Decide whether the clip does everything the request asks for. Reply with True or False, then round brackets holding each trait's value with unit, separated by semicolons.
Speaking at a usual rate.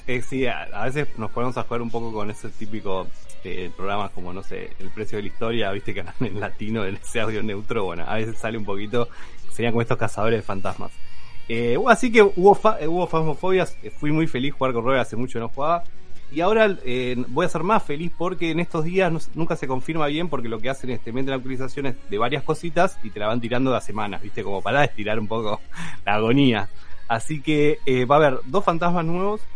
False (235 wpm)